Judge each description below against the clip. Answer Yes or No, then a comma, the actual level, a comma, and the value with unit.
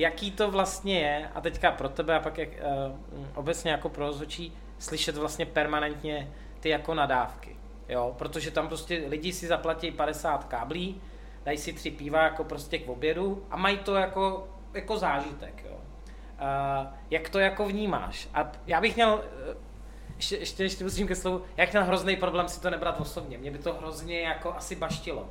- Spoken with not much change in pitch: No, average, 3.7 semitones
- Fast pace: Yes, fast, 180 wpm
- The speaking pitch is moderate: Yes, medium, 165 Hz